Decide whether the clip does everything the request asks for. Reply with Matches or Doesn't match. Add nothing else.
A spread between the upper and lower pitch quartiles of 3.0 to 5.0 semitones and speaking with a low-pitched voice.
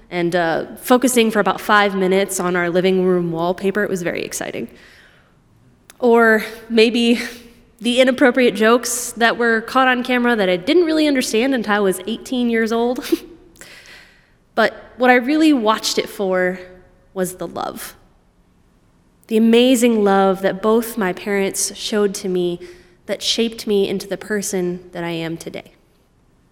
Doesn't match